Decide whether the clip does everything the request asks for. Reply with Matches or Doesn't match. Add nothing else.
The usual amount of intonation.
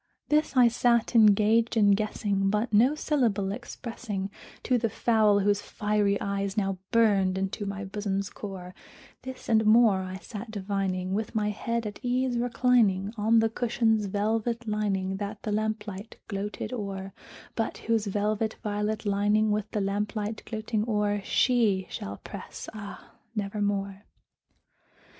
Doesn't match